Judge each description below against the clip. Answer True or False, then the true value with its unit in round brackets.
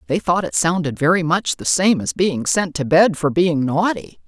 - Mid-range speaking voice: True (160 Hz)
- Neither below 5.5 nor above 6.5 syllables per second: False (4.7 syllables/s)